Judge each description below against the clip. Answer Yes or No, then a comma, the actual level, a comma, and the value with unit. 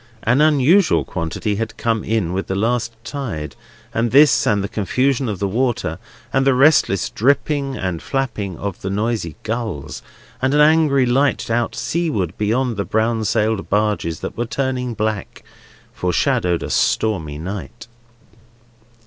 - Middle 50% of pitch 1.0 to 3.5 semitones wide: No, average, 5.0 semitones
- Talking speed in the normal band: Yes, average, 150 wpm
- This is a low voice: Yes, low, 115 Hz